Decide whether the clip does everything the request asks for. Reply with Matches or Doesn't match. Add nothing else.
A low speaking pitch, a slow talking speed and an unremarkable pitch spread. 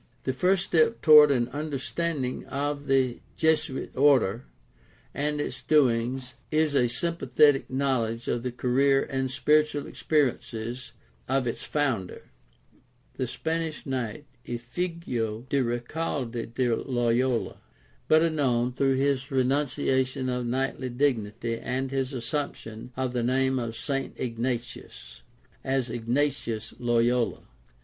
Matches